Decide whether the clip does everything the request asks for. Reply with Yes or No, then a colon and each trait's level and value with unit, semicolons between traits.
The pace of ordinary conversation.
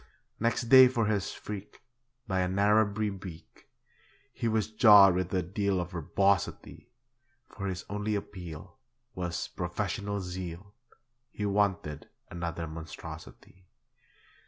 No: slow, 115 wpm